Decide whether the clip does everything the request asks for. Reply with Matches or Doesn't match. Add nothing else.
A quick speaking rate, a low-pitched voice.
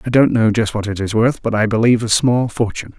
Matches